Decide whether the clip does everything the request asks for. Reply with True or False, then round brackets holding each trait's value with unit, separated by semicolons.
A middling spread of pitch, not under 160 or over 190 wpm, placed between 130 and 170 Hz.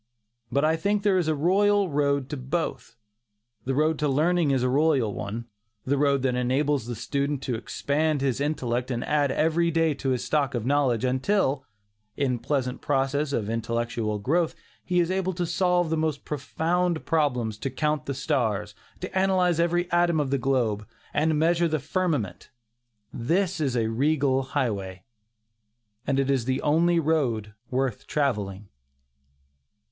True (4.3 semitones; 165 wpm; 140 Hz)